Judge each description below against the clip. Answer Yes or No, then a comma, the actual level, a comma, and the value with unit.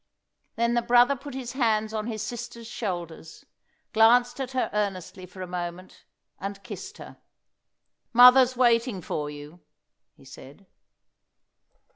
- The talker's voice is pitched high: Yes, high, 220 Hz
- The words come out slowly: Yes, slow, 130 wpm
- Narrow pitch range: No, average, 4.9 semitones